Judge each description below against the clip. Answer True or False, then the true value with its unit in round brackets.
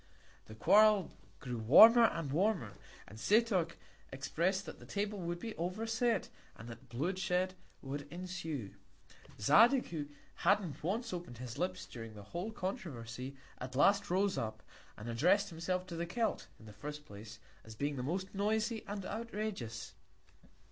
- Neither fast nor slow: True (155 wpm)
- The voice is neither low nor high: True (175 Hz)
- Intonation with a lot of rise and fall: True (8.2 semitones)